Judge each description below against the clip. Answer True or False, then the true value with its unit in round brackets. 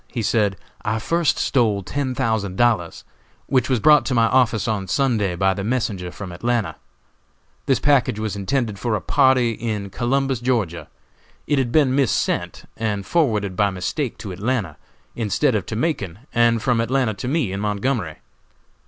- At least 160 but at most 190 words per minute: True (165 wpm)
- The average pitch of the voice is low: True (115 Hz)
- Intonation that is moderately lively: True (4.4 semitones)